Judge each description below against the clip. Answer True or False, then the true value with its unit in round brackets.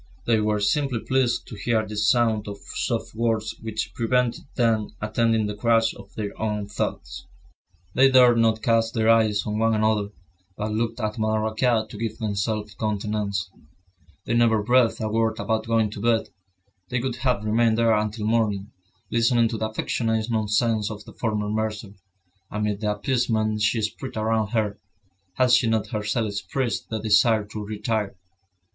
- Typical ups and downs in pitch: False (1.6 semitones)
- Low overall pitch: True (110 Hz)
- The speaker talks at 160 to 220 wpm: True (165 wpm)